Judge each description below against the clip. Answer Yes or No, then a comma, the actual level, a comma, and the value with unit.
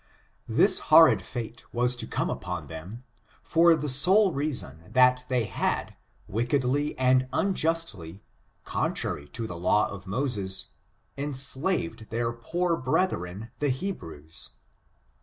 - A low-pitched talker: Yes, low, 125 Hz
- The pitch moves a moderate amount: No, wide, 6.6 semitones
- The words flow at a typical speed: No, slow, 120 wpm